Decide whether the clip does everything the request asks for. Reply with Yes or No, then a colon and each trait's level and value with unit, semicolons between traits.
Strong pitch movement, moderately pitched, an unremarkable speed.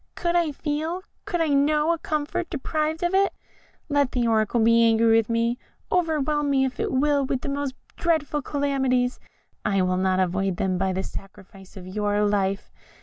No: wide, 6.5 semitones; very high, 265 Hz; average, 180 wpm